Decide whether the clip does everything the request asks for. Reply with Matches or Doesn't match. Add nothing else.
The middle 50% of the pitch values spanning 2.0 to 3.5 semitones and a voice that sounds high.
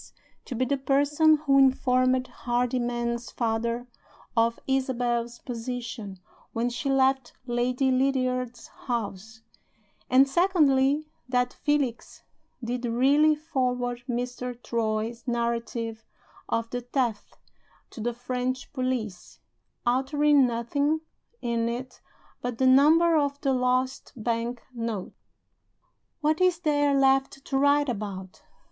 Matches